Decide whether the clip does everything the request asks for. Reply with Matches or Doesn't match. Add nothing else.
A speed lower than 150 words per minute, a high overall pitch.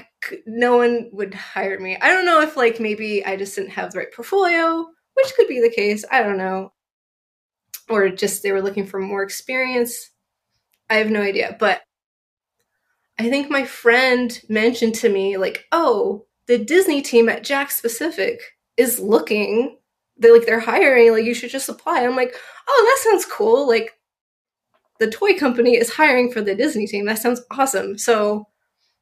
Doesn't match